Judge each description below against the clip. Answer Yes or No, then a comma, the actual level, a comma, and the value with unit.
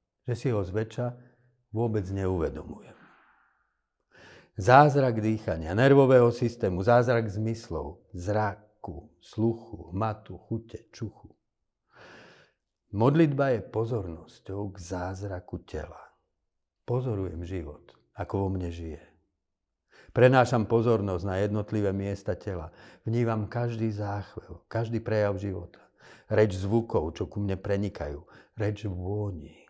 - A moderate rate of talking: No, slow, 100 wpm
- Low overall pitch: Yes, low, 105 Hz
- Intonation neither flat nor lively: Yes, average, 3.7 semitones